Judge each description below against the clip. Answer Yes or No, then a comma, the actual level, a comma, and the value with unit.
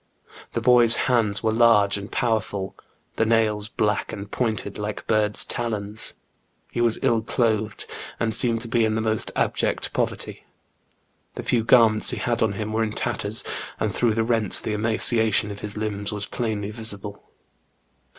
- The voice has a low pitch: Yes, low, 110 Hz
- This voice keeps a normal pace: Yes, average, 165 wpm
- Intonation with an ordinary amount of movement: No, narrow, 1.6 semitones